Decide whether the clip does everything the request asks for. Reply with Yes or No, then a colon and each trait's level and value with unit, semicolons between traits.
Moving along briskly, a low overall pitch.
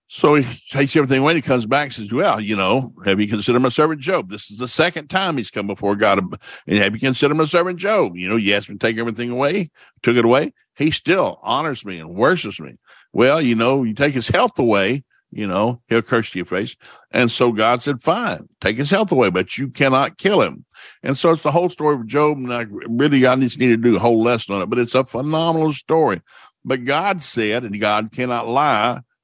Yes: fast, 240 wpm; low, 125 Hz